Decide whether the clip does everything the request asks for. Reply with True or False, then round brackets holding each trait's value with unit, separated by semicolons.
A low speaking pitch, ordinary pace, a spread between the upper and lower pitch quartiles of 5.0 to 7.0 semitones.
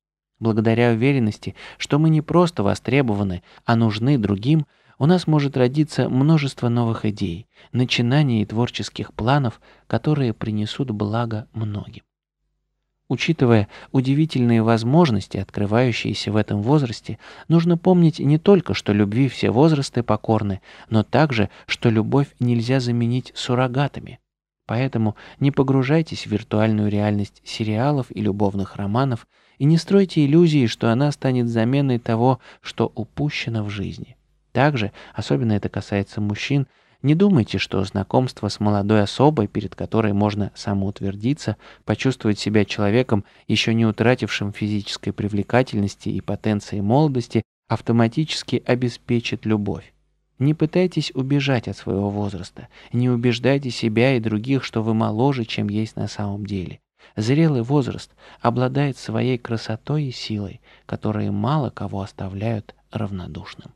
False (115 Hz; 125 wpm; 4.4 semitones)